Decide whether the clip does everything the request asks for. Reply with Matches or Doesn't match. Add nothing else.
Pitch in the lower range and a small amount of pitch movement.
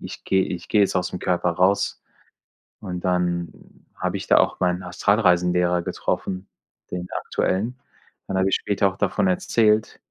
Matches